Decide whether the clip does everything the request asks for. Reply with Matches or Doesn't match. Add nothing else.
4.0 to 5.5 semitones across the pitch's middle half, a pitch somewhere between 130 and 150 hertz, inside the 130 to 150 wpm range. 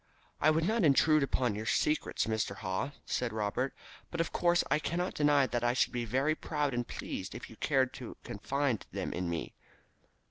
Doesn't match